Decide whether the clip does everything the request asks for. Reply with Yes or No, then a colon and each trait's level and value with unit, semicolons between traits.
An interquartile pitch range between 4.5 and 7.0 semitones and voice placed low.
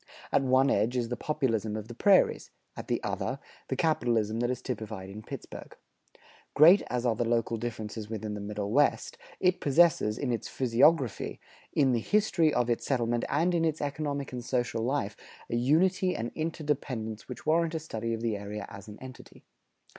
Yes: average, 5.1 semitones; low, 120 Hz